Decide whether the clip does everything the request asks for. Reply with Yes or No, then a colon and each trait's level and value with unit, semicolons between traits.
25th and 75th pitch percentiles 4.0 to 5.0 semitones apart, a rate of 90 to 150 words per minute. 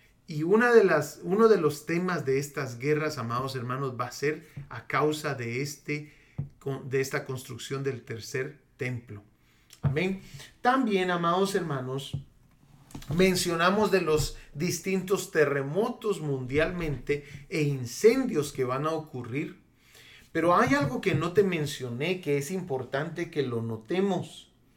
Yes: average, 4.7 semitones; average, 135 wpm